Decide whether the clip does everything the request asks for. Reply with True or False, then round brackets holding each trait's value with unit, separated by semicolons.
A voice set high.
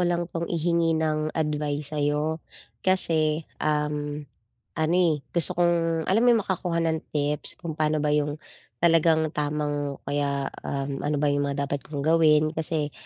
False (155 Hz)